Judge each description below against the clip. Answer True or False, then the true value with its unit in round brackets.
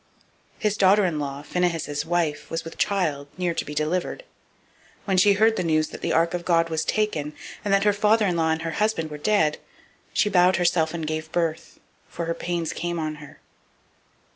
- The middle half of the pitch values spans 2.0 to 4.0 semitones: True (3.1 semitones)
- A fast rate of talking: True (210 wpm)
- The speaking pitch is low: False (170 Hz)